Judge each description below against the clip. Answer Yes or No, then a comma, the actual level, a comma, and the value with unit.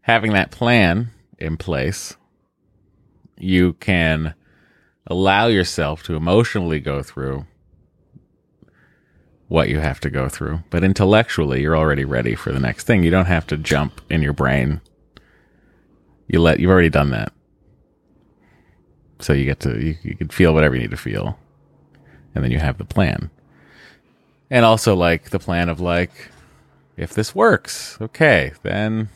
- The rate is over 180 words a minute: No, average, 150 wpm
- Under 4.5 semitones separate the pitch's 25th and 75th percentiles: No, average, 4.8 semitones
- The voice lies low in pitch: Yes, very low, 85 Hz